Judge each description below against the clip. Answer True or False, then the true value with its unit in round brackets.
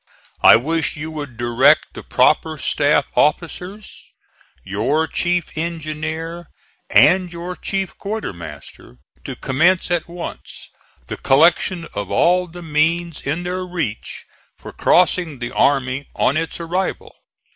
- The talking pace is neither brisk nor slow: False (125 wpm)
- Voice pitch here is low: False (160 Hz)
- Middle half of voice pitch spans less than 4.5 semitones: True (3.9 semitones)